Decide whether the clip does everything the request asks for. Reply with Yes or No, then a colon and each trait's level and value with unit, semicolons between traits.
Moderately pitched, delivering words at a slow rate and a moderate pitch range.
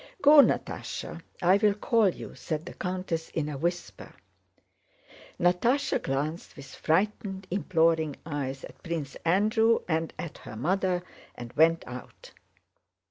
Yes: medium, 170 Hz; slow, 130 wpm; average, 3.9 semitones